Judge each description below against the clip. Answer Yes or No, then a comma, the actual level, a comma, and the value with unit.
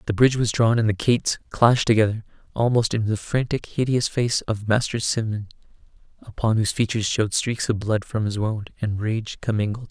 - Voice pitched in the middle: No, low, 110 Hz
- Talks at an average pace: Yes, average, 190 wpm